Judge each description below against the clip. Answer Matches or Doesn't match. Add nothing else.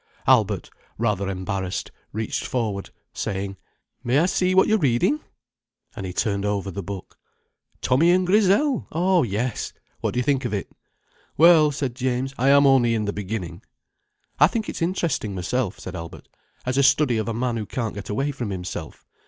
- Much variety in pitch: Matches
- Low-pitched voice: Matches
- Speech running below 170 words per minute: Doesn't match